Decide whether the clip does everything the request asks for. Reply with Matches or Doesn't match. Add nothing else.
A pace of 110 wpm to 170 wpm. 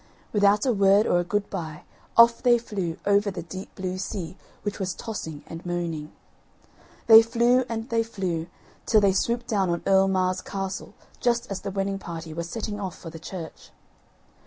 Doesn't match